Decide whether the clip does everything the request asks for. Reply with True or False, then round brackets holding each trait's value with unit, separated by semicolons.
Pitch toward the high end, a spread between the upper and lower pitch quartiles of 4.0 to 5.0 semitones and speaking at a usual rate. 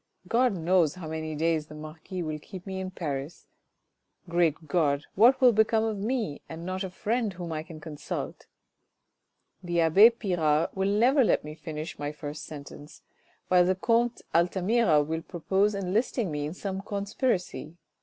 False (175 Hz; 4.6 semitones; 165 wpm)